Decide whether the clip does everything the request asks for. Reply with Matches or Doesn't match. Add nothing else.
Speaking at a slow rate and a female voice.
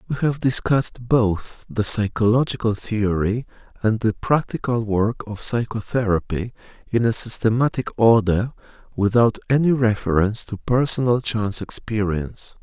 Doesn't match